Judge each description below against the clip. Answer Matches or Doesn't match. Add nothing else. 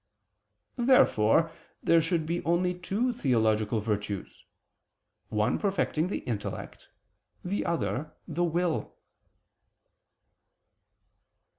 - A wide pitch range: Matches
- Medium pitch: Matches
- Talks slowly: Matches